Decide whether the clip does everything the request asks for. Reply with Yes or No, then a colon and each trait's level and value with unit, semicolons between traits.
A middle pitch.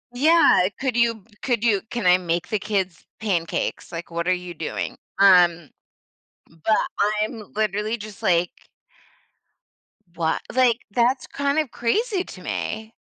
No: high, 210 Hz